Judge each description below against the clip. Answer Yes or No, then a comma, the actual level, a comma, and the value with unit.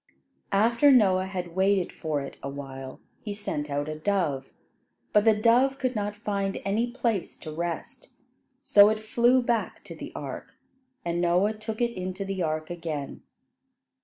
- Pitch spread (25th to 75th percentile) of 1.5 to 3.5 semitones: No, average, 4.8 semitones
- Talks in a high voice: Yes, high, 195 Hz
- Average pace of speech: Yes, average, 160 wpm